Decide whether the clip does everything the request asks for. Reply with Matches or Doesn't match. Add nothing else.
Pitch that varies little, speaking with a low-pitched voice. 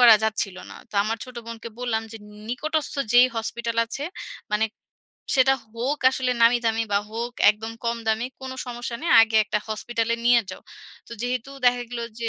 Doesn't match